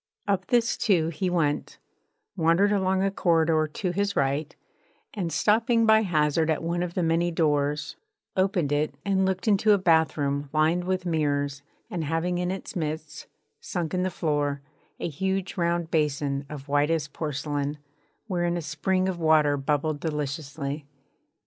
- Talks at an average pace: Yes, average, 155 wpm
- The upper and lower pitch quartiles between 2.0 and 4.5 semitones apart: Yes, average, 3.8 semitones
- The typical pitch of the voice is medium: Yes, medium, 165 Hz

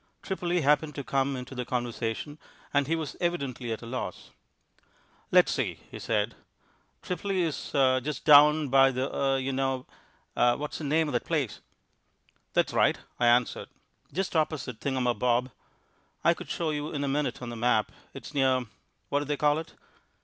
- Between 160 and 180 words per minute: Yes, average, 170 wpm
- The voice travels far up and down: No, average, 3.1 semitones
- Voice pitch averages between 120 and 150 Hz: Yes, low, 135 Hz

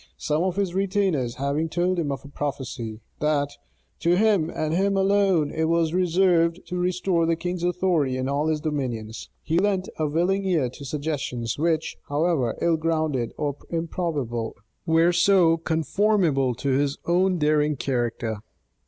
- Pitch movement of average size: Yes, average, 4.0 semitones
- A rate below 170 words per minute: Yes, average, 155 wpm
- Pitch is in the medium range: Yes, medium, 160 Hz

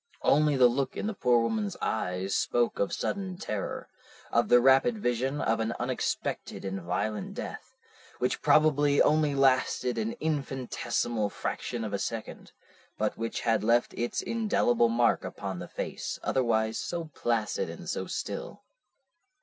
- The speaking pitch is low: Yes, low, 125 Hz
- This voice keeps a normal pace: Yes, average, 150 wpm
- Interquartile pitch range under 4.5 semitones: No, average, 5.0 semitones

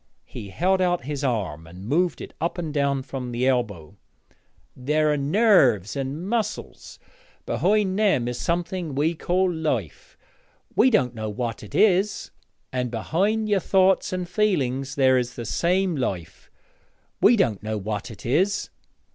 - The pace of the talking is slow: No, average, 155 wpm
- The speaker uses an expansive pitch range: Yes, wide, 7.4 semitones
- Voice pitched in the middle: Yes, medium, 145 Hz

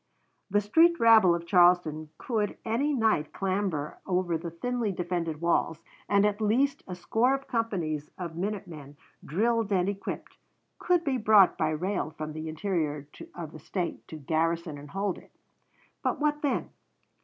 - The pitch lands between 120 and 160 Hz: No, medium, 185 Hz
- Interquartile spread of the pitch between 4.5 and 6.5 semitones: Yes, wide, 5.4 semitones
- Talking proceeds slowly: No, average, 160 wpm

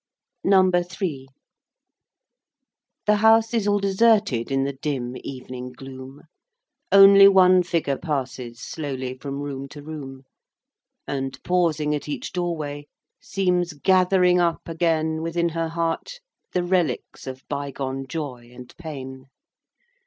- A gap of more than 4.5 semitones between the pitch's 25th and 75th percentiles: Yes, average, 5.2 semitones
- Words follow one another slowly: Yes, slow, 125 wpm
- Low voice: No, medium, 155 Hz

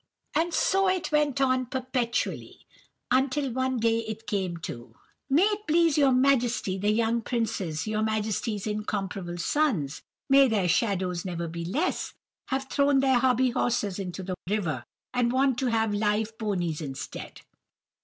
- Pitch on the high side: Yes, high, 230 Hz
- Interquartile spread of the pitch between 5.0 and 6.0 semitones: Yes, average, 5.3 semitones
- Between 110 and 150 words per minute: Yes, average, 140 wpm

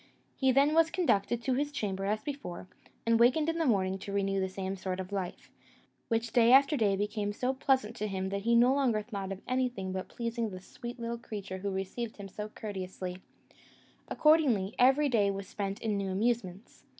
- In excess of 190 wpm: Yes, average, 200 wpm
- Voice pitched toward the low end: No, high, 215 Hz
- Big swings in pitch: No, average, 4.3 semitones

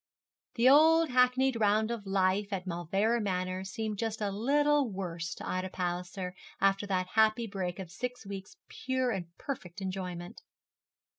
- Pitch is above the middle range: Yes, high, 200 Hz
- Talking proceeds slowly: No, average, 155 wpm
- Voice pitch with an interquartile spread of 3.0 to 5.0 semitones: Yes, average, 4.2 semitones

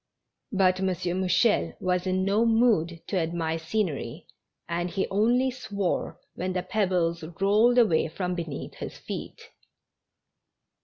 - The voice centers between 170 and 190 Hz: Yes, medium, 185 Hz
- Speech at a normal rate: No, slow, 125 wpm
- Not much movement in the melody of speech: No, average, 3.3 semitones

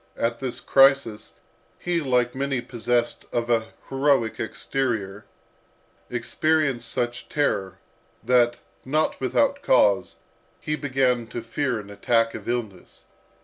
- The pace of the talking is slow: Yes, slow, 115 wpm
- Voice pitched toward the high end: No, low, 125 Hz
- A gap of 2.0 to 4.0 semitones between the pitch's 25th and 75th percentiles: Yes, average, 2.9 semitones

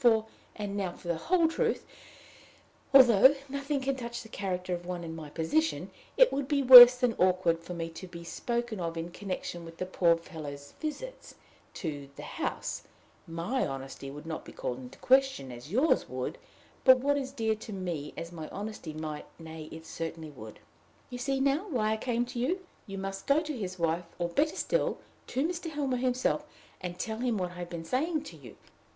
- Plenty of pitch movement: Yes, wide, 8.0 semitones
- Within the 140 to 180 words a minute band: No, average, 200 wpm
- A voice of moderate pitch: No, high, 195 Hz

